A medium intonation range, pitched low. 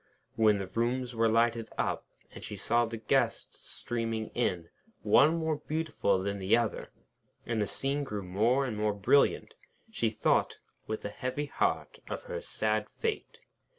Yes: average, 3.5 semitones; low, 115 Hz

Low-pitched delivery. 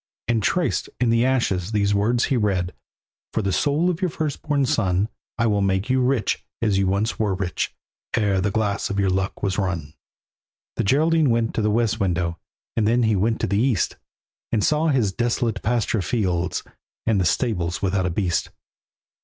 Yes: low, 105 Hz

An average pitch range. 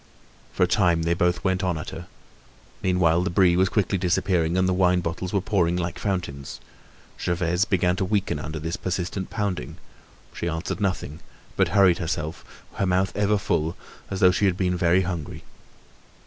No: narrow, 1.8 semitones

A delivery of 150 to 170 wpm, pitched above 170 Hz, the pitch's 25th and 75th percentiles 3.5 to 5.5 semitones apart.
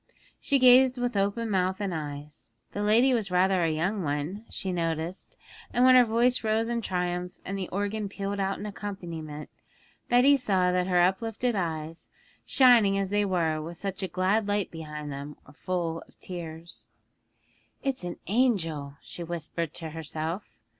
Yes: average, 165 wpm; medium, 185 Hz; average, 4.5 semitones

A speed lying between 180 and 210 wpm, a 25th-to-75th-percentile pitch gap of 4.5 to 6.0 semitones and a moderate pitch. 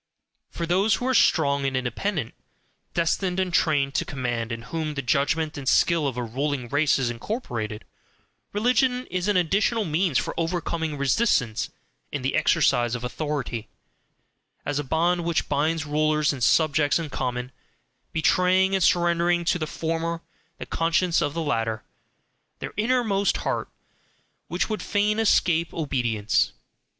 No: average, 145 wpm; average, 4.9 semitones; medium, 155 Hz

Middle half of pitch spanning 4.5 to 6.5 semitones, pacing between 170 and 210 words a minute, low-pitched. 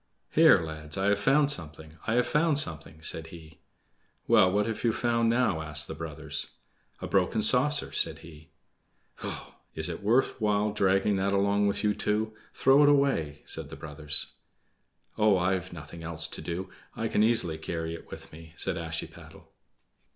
Yes: wide, 5.5 semitones; average, 175 wpm; very low, 95 Hz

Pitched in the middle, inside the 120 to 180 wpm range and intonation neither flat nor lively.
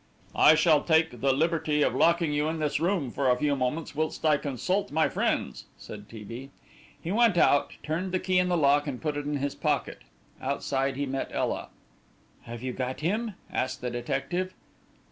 No: medium, 150 Hz; average, 195 wpm; average, 3.6 semitones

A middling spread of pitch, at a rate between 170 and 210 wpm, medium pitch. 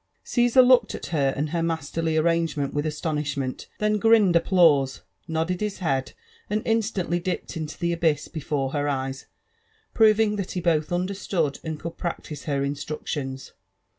No: average, 4.3 semitones; average, 155 wpm; medium, 165 Hz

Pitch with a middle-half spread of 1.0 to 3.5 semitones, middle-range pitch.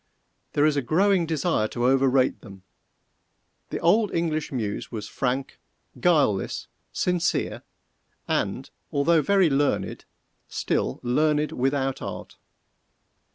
No: average, 4.5 semitones; medium, 145 Hz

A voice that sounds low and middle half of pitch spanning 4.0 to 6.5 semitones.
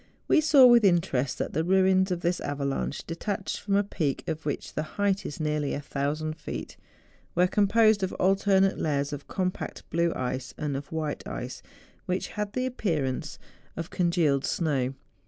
No: medium, 170 Hz; average, 5.0 semitones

